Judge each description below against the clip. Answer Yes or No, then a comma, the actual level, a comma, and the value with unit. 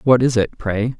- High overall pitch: No, low, 115 Hz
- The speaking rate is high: Yes, fast, 240 wpm